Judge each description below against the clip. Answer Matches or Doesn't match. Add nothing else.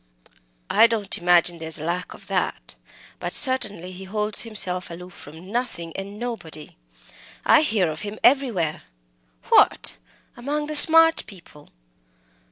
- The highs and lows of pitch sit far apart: Matches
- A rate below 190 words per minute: Matches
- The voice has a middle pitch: Doesn't match